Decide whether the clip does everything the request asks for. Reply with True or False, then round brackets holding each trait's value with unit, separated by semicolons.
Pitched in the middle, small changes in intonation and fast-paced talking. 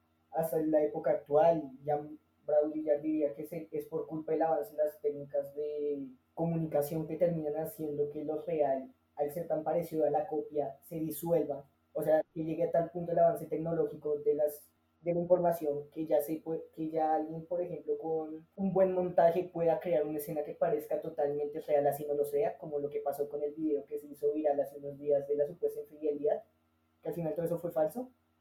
True (150 Hz; 1.7 semitones; 210 wpm)